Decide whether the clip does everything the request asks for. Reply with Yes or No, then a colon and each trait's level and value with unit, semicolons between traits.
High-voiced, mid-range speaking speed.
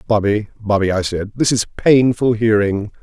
No: low, 110 Hz; average, 160 wpm